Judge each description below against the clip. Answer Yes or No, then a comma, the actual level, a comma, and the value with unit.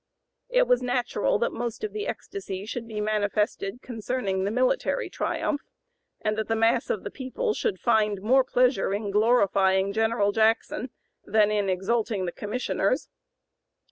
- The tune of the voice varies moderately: Yes, average, 3.6 semitones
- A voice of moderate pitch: No, high, 220 Hz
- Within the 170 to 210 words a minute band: No, average, 150 wpm